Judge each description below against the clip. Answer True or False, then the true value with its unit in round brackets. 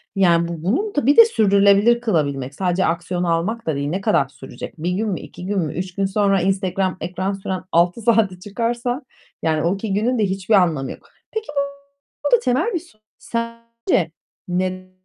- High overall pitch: True (195 Hz)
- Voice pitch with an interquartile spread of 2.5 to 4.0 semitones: False (4.6 semitones)